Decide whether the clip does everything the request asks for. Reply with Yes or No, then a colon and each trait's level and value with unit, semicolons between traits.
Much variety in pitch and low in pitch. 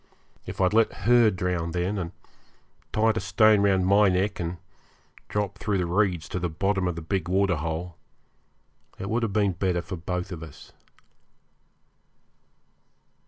No: average, 2.7 semitones; very low, 95 Hz